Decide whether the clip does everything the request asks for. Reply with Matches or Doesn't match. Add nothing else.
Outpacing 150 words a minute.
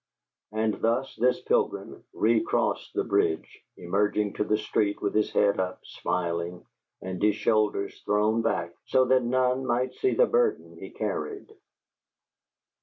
Doesn't match